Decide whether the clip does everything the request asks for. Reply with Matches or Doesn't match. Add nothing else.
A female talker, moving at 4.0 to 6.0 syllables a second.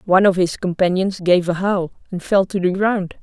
Matches